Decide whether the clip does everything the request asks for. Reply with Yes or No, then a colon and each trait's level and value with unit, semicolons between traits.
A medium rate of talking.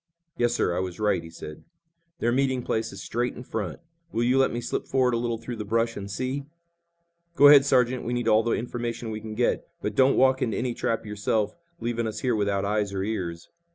No: fast, 225 wpm